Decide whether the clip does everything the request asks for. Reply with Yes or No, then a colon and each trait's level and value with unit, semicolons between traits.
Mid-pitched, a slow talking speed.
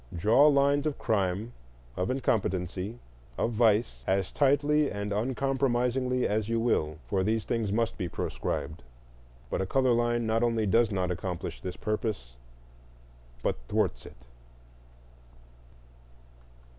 No: low, 115 Hz; slow, 125 wpm